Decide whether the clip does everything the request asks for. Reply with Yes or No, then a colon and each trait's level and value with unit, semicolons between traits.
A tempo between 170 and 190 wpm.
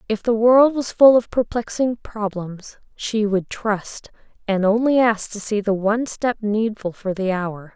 Yes: average, 180 wpm